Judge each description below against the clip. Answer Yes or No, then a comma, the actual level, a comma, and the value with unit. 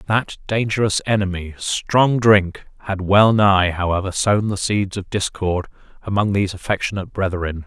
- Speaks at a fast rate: No, average, 140 wpm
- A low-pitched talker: Yes, low, 100 Hz